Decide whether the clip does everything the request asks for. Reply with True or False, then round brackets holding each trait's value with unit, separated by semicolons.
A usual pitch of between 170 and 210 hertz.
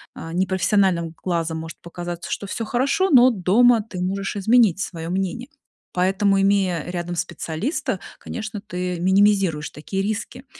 True (190 Hz)